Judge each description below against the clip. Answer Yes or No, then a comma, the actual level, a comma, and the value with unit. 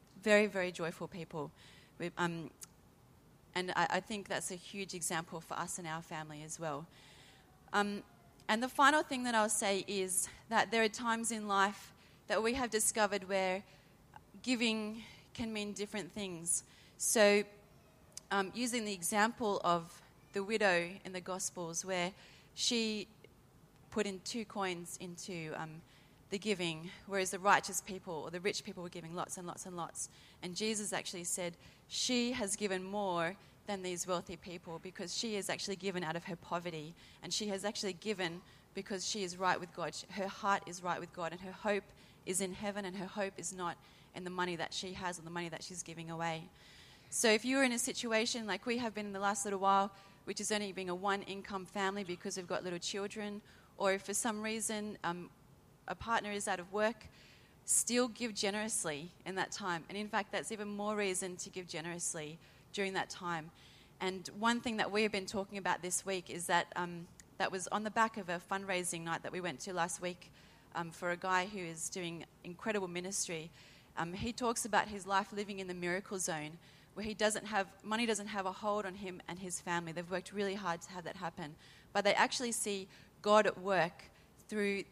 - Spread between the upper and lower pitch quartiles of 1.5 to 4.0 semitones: Yes, average, 3.0 semitones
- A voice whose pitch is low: No, high, 190 Hz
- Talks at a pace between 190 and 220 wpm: Yes, average, 200 wpm